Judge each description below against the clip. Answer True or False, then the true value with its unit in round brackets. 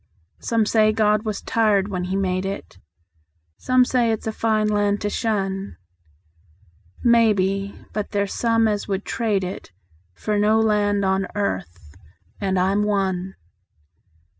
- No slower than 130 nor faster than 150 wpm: True (140 wpm)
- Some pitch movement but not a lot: False (2.0 semitones)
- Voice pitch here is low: False (205 Hz)